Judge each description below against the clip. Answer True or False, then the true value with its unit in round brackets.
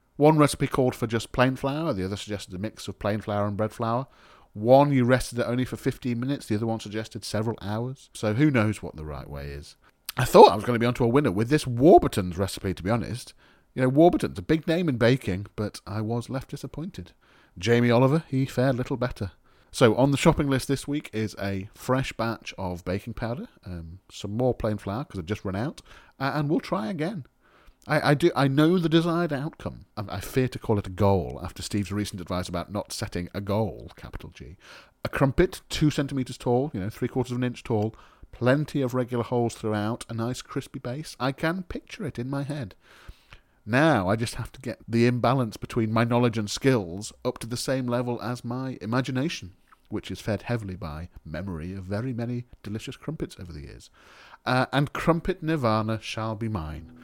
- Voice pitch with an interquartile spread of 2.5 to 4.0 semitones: False (4.5 semitones)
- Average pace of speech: False (215 wpm)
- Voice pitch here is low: True (120 Hz)